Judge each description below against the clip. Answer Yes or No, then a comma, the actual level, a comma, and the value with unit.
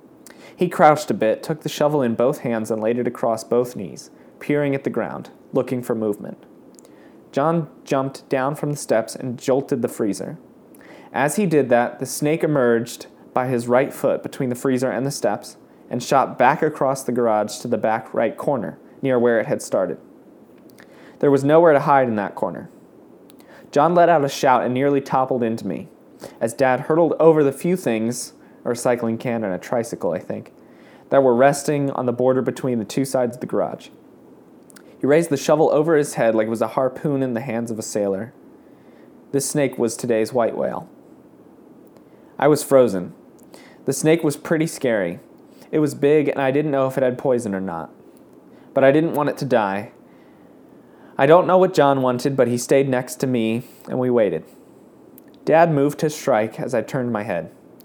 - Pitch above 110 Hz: Yes, low, 135 Hz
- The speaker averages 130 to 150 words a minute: No, average, 195 wpm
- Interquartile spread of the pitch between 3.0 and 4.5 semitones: Yes, average, 3.3 semitones